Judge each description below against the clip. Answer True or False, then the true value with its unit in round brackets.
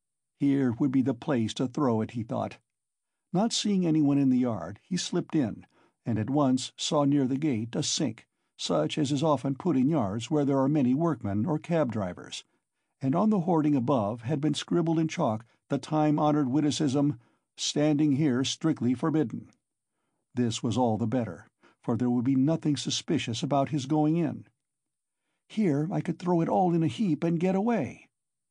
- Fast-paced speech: False (185 wpm)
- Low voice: False (145 Hz)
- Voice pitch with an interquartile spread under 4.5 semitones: True (3.9 semitones)